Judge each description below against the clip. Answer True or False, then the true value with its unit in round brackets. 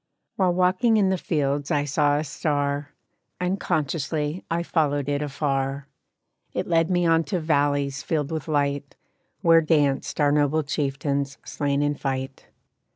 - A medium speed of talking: True (145 wpm)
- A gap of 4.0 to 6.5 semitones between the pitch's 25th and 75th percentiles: False (2.5 semitones)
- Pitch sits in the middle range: True (145 Hz)